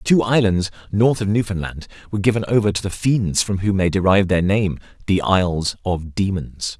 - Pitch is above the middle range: No, low, 100 Hz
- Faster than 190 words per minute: No, average, 185 wpm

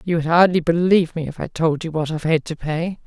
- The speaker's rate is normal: No, fast, 275 wpm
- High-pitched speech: No, medium, 165 Hz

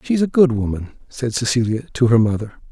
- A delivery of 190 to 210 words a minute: Yes, average, 200 wpm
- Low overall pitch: Yes, low, 125 Hz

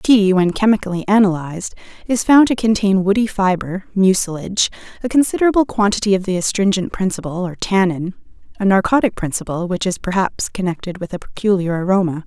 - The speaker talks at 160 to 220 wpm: No, average, 150 wpm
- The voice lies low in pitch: No, high, 195 Hz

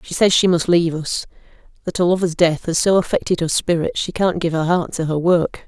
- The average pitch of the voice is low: No, medium, 170 Hz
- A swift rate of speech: Yes, fast, 245 wpm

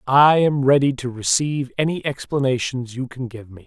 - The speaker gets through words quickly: No, average, 180 wpm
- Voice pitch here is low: Yes, low, 130 Hz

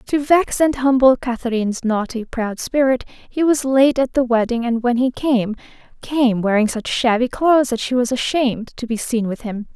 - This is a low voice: No, high, 245 Hz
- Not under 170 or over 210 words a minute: Yes, average, 195 wpm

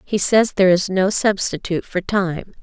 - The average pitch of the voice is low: No, high, 190 Hz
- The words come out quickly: No, average, 185 wpm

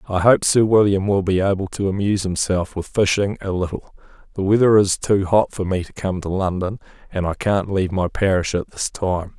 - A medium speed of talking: No, fast, 215 wpm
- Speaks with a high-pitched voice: No, very low, 95 Hz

